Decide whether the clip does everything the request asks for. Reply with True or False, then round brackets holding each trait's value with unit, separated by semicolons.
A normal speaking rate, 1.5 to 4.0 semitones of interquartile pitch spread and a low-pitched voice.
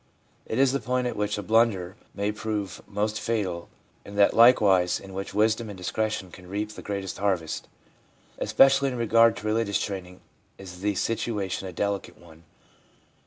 True (165 wpm; 2.9 semitones; 105 Hz)